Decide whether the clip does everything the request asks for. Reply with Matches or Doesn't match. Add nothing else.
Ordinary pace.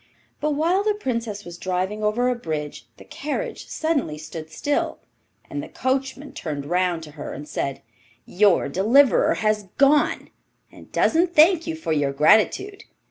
Matches